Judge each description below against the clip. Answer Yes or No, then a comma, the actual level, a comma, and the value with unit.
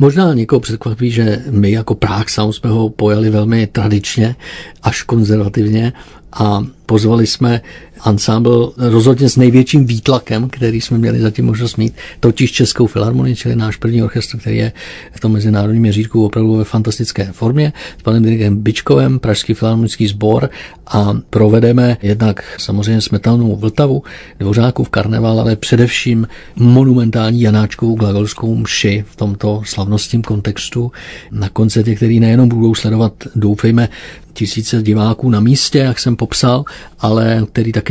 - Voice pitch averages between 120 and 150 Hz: No, low, 110 Hz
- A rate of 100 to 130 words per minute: No, average, 140 wpm